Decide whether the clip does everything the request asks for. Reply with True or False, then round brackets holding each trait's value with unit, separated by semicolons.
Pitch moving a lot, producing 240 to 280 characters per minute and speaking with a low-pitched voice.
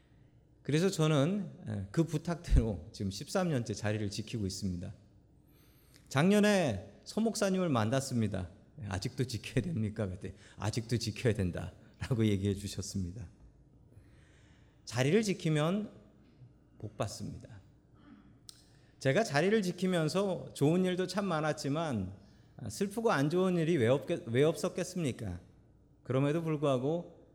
True (7.7 semitones; 265 characters per minute; 130 Hz)